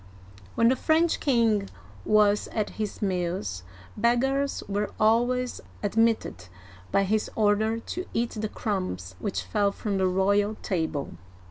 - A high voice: Yes, high, 210 Hz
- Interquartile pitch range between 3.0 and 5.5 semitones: Yes, average, 3.3 semitones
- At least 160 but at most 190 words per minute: No, slow, 135 wpm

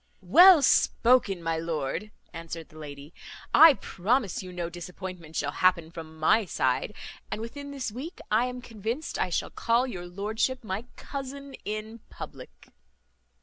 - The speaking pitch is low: No, high, 200 Hz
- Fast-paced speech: No, average, 145 wpm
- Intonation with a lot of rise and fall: Yes, wide, 6.9 semitones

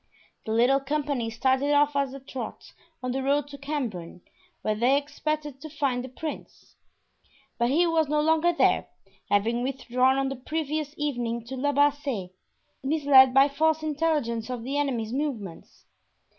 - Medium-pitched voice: No, very high, 275 Hz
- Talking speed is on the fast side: No, average, 155 wpm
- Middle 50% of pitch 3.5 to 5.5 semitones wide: No, average, 3.0 semitones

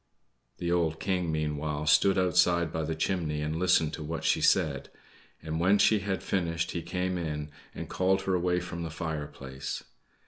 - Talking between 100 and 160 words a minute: No, average, 175 wpm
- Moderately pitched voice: No, very low, 85 Hz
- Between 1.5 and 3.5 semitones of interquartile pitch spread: Yes, average, 2.8 semitones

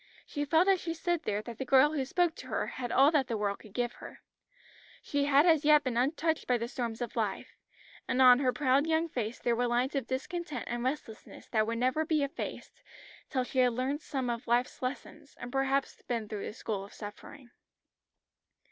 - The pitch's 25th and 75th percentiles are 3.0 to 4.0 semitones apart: Yes, average, 3.6 semitones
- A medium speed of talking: No, fast, 210 wpm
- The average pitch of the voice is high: Yes, very high, 260 Hz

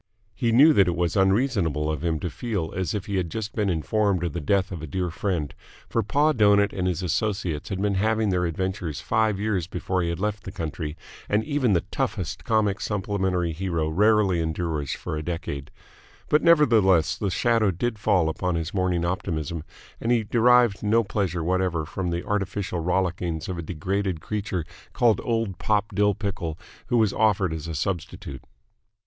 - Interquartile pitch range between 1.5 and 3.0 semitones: No, average, 3.8 semitones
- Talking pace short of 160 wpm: No, average, 185 wpm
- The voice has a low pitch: Yes, very low, 95 Hz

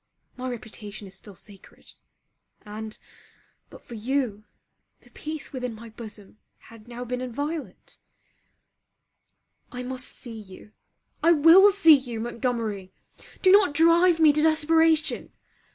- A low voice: No, very high, 250 Hz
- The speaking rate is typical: No, slow, 125 wpm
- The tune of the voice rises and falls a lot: Yes, wide, 6.2 semitones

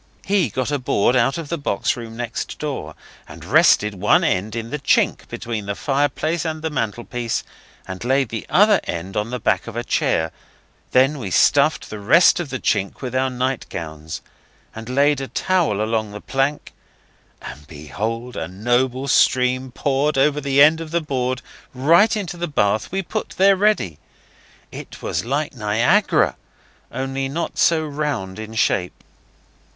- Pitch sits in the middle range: No, low, 130 Hz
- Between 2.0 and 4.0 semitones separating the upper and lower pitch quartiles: No, wide, 5.4 semitones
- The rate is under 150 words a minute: No, average, 165 wpm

